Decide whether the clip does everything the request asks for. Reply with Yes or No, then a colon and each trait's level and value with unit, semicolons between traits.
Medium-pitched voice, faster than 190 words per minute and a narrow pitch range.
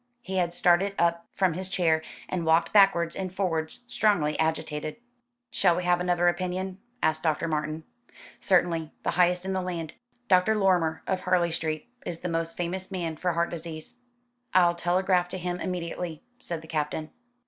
No: medium, 175 Hz; average, 170 wpm; narrow, 2.2 semitones